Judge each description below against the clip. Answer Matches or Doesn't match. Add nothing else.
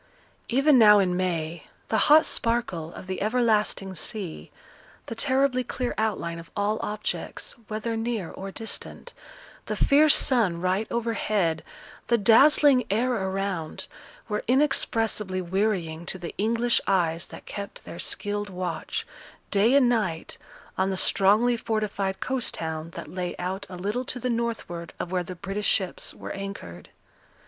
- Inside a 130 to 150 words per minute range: Matches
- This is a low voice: Doesn't match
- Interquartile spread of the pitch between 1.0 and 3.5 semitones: Doesn't match